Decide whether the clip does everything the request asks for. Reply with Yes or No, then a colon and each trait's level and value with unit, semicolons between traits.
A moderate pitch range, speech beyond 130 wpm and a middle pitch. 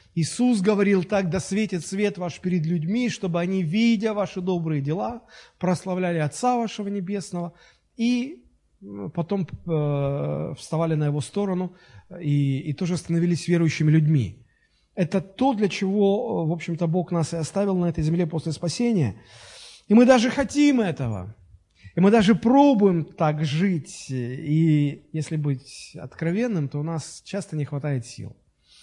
Yes: average, 4.9 semitones; average, 140 wpm; medium, 175 Hz